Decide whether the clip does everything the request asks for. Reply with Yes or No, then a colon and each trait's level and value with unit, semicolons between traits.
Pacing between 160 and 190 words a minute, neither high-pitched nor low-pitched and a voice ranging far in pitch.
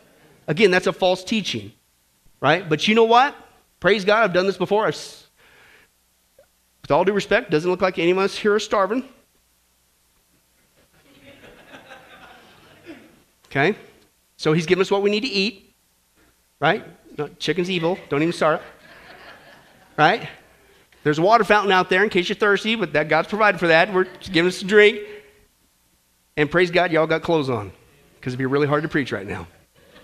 Yes: average, 175 wpm; medium, 175 Hz; wide, 8.9 semitones